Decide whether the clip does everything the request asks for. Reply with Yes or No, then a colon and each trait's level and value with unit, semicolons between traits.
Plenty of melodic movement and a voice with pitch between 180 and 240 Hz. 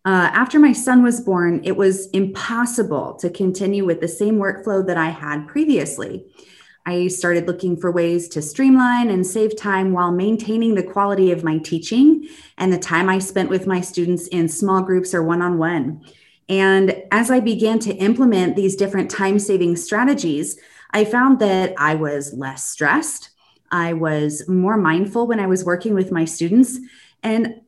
No: average, 3.9 semitones; high, 190 Hz